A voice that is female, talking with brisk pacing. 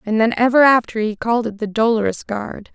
Yes: female; fast, 220 wpm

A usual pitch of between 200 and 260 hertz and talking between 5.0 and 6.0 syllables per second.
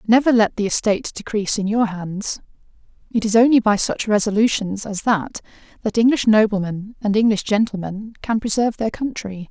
Yes: high, 215 Hz; 5.4 syllables/s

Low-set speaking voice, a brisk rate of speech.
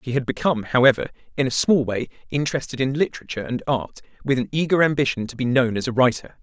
Yes: low, 130 Hz; fast, 215 wpm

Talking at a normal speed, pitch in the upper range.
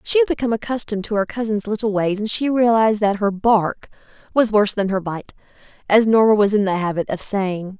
No: fast, 215 wpm; high, 210 Hz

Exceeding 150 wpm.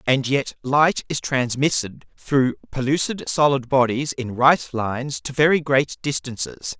No: average, 140 wpm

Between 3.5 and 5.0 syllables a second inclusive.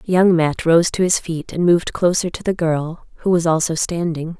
Yes: 4.9 syllables/s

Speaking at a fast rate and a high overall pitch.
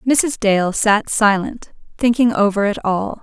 No: average, 150 wpm; high, 215 Hz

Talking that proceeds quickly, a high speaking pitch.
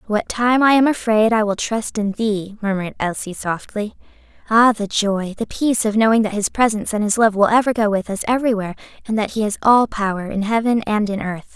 Yes: fast, 225 wpm; high, 215 Hz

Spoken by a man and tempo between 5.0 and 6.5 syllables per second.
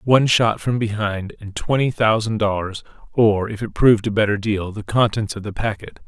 Yes: male; 5.2 syllables/s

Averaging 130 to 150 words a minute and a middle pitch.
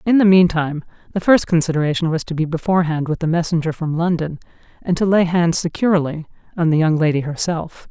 No: average, 190 wpm; medium, 165 Hz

